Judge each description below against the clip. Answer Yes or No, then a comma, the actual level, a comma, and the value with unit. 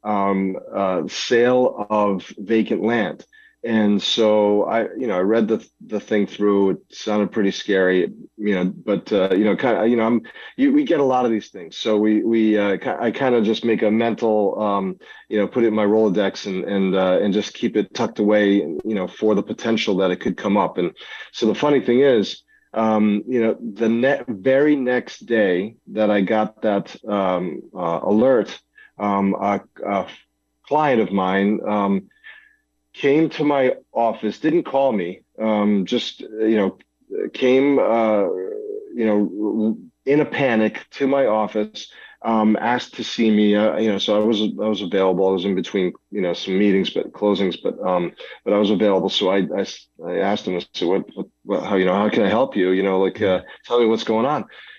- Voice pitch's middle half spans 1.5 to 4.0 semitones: Yes, average, 2.7 semitones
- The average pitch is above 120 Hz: No, low, 110 Hz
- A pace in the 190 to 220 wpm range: Yes, fast, 205 wpm